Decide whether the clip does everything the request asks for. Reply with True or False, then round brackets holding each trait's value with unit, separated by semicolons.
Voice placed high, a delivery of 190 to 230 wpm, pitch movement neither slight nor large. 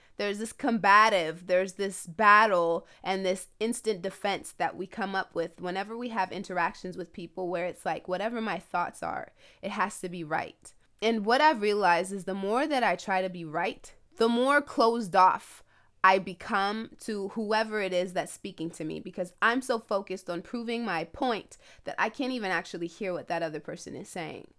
True (195 Hz; 195 wpm; 3.6 semitones)